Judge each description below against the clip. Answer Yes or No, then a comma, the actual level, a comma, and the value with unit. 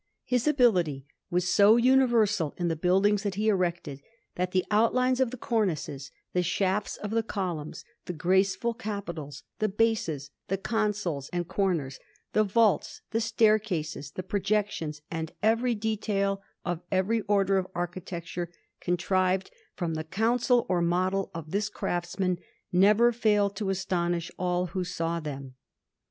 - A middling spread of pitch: Yes, average, 3.7 semitones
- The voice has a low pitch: No, high, 190 Hz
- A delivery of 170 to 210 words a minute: No, average, 145 wpm